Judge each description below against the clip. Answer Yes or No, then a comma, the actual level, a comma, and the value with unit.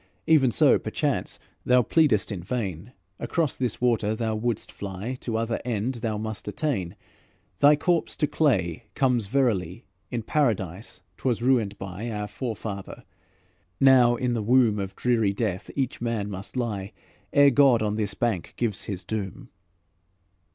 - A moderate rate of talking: Yes, average, 150 wpm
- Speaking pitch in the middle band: No, low, 115 Hz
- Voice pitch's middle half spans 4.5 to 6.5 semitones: No, average, 3.9 semitones